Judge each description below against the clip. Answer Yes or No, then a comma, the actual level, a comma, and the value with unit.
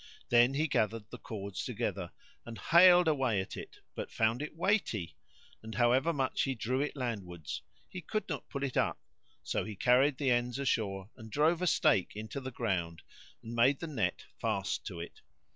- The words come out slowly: No, average, 185 wpm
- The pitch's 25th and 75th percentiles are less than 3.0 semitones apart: No, average, 4.9 semitones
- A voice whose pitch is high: No, low, 120 Hz